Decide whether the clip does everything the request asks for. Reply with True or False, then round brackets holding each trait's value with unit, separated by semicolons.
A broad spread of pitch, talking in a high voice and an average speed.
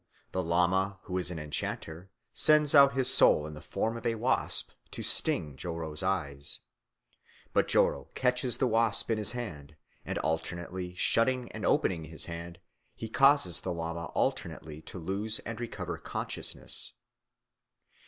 False (5.8 semitones; 90 Hz; 155 wpm)